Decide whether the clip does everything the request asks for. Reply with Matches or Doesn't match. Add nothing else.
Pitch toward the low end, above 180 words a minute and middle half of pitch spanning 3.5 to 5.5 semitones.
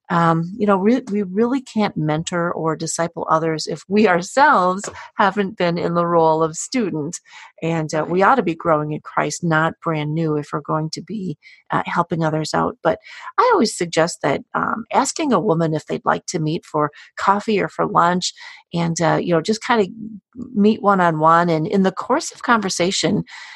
Doesn't match